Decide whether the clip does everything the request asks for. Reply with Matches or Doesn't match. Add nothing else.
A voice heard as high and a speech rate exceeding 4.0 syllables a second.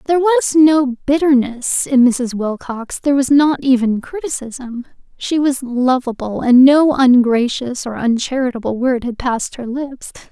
Matches